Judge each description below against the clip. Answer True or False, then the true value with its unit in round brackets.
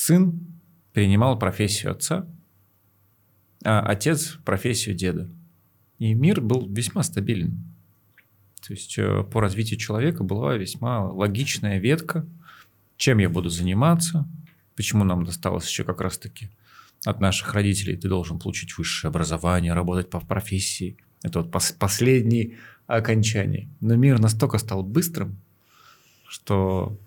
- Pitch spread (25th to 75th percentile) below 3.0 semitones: False (4.2 semitones)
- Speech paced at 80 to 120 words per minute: True (115 wpm)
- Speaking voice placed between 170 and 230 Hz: False (105 Hz)